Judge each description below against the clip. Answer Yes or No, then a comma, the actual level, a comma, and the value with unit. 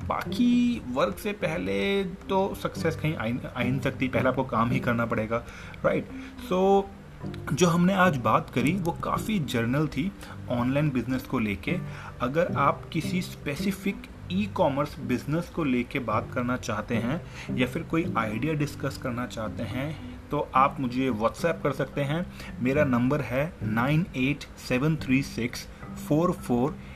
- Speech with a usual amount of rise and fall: No, wide, 5.8 semitones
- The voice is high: No, low, 135 Hz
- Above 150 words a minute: Yes, average, 160 wpm